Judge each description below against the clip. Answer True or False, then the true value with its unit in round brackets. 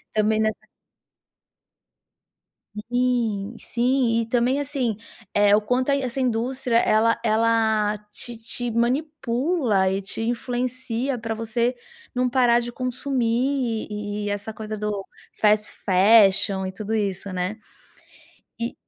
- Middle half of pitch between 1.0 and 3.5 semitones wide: True (2.8 semitones)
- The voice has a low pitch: False (230 Hz)